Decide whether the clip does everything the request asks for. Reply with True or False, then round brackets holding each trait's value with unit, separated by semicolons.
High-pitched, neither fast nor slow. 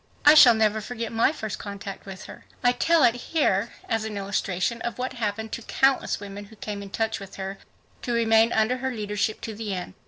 False (220 Hz; 215 wpm)